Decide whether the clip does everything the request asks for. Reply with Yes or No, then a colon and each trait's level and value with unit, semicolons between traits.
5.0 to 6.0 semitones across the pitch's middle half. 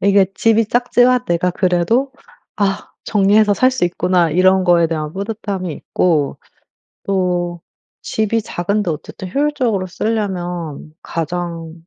No: average, 3.8 semitones